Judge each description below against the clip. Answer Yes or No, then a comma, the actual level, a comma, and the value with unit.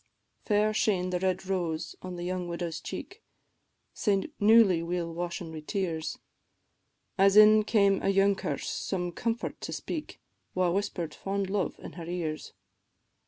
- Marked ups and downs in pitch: No, average, 2.8 semitones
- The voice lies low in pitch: No, medium, 185 Hz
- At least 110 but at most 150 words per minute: Yes, average, 145 wpm